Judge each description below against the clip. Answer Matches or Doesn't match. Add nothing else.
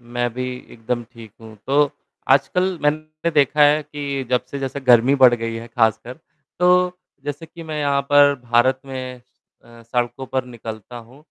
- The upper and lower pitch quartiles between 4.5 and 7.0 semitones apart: Doesn't match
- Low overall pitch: Matches